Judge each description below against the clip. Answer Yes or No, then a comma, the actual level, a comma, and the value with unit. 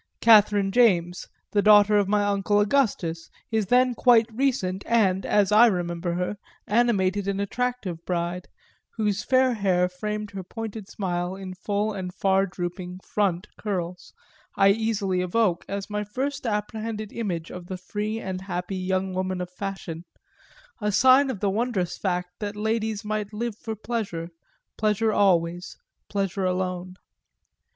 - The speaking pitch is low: No, high, 200 Hz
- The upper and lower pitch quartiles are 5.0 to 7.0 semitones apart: No, average, 2.9 semitones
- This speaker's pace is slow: No, average, 145 wpm